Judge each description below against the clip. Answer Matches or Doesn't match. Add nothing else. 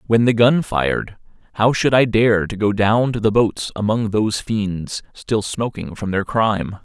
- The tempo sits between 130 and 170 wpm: Doesn't match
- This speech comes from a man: Matches